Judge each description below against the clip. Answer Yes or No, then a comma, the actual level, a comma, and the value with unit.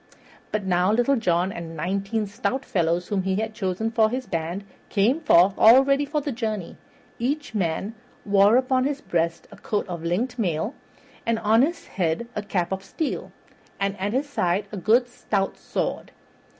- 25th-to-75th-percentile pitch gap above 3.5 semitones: Yes, average, 5.0 semitones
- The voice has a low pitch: No, high, 210 Hz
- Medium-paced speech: Yes, average, 175 wpm